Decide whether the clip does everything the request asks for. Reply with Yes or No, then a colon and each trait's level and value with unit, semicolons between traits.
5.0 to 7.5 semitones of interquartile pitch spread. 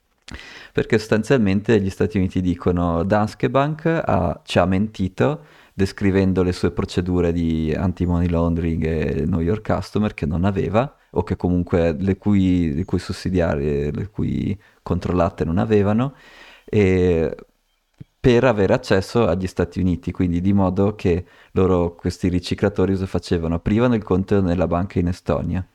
No: narrow, 2.6 semitones